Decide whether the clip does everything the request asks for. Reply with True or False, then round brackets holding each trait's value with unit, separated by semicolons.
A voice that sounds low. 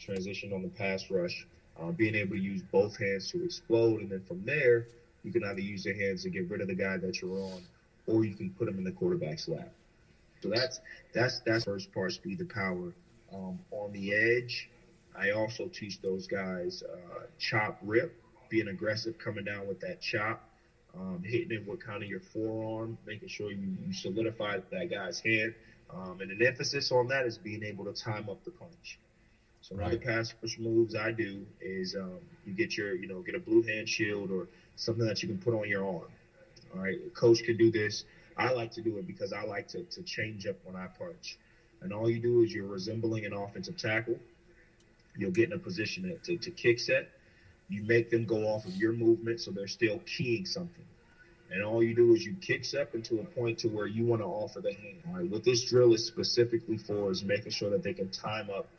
True (115 Hz)